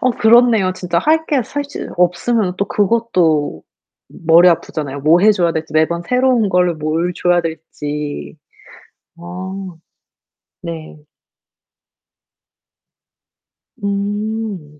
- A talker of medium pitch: Yes, medium, 180 Hz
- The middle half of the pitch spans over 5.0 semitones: Yes, wide, 5.4 semitones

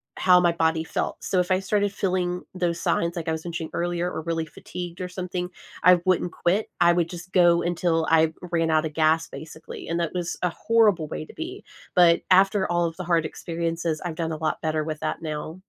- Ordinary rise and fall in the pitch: No, narrow, 1.9 semitones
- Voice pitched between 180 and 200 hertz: No, medium, 170 Hz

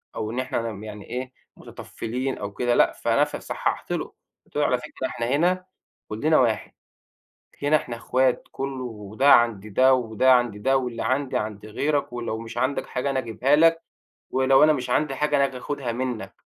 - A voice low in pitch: Yes, low, 125 Hz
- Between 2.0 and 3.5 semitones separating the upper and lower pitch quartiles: Yes, average, 3.1 semitones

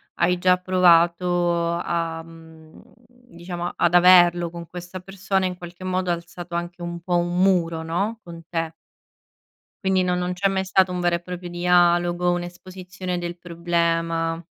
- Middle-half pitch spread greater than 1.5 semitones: No, narrow, 1.1 semitones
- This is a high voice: No, medium, 175 Hz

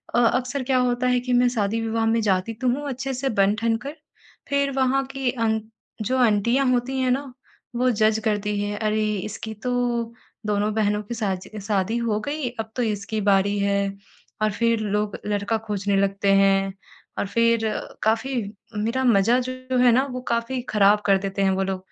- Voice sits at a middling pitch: No, high, 225 Hz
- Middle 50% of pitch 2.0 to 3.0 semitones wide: No, average, 3.5 semitones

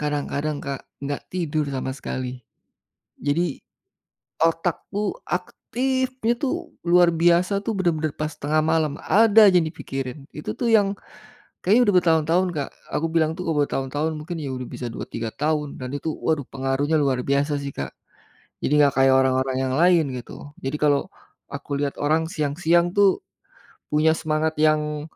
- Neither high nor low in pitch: Yes, medium, 155 Hz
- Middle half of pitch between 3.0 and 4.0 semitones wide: Yes, average, 3.4 semitones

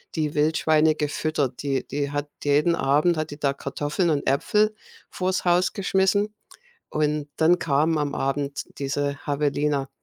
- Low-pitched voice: No, medium, 150 Hz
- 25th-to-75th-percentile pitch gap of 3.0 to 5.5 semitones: No, narrow, 2.5 semitones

